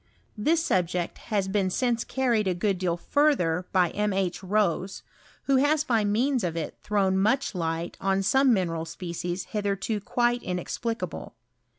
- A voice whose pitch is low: No, high, 200 Hz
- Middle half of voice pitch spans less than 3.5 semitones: No, average, 4.7 semitones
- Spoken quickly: No, average, 150 wpm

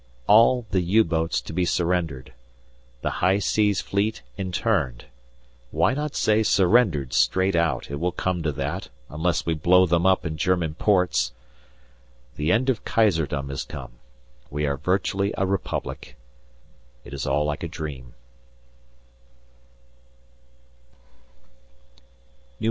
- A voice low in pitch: Yes, very low, 90 Hz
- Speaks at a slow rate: Yes, slow, 125 wpm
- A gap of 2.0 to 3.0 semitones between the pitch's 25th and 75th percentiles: No, average, 4.7 semitones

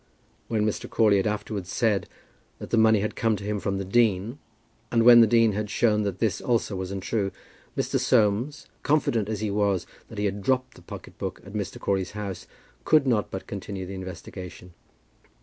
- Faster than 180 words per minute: Yes, average, 195 wpm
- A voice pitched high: No, low, 105 Hz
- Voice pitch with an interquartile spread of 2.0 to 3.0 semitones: Yes, narrow, 2.5 semitones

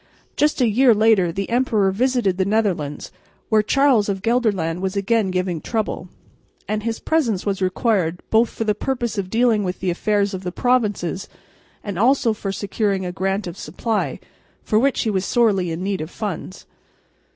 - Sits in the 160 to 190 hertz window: No, high, 205 Hz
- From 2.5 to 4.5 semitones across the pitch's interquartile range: Yes, average, 3.4 semitones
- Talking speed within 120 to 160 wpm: No, average, 175 wpm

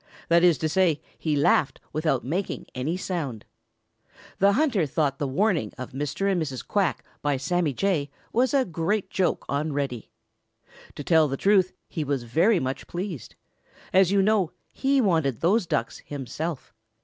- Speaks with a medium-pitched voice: Yes, medium, 165 Hz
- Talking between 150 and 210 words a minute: Yes, average, 160 wpm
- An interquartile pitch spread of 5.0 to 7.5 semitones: Yes, average, 5.3 semitones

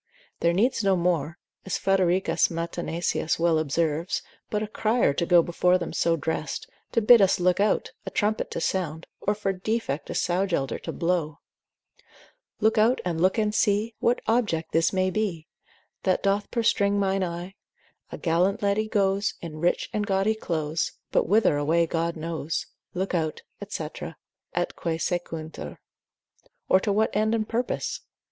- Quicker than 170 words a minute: No, average, 165 wpm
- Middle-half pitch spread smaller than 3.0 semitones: No, average, 3.9 semitones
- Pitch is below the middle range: No, medium, 185 Hz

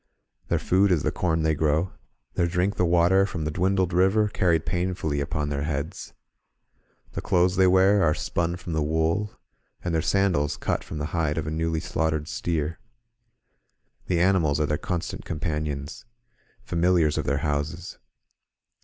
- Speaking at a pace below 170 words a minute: Yes, average, 160 wpm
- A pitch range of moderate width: Yes, average, 3.0 semitones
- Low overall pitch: Yes, very low, 85 Hz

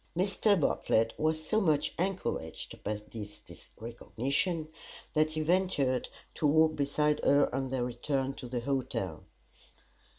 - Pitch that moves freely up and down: No, average, 3.7 semitones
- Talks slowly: Yes, slow, 130 wpm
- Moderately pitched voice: Yes, medium, 145 Hz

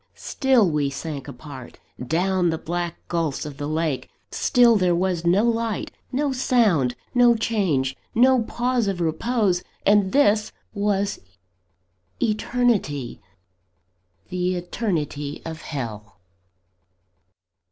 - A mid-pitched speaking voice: Yes, medium, 180 Hz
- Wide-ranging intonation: Yes, wide, 6.8 semitones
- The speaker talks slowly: Yes, slow, 110 wpm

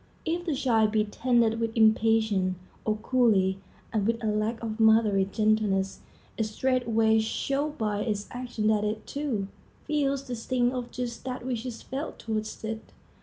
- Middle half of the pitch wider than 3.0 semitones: No, average, 2.7 semitones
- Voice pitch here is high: Yes, high, 225 Hz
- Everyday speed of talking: Yes, average, 165 wpm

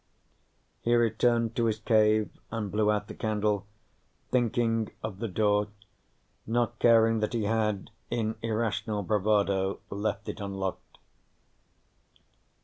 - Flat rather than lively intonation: Yes, narrow, 1.7 semitones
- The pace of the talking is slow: Yes, slow, 120 wpm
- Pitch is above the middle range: No, low, 110 Hz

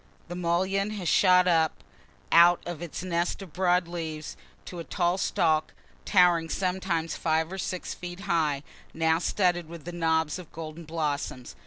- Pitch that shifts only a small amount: Yes, narrow, 2.0 semitones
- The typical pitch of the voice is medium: Yes, medium, 170 Hz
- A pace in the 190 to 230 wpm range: No, average, 155 wpm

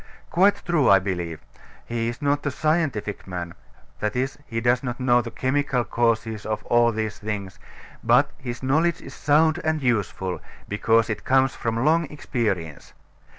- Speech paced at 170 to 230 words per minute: No, average, 160 wpm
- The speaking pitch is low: Yes, low, 120 Hz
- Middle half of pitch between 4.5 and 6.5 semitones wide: Yes, average, 4.9 semitones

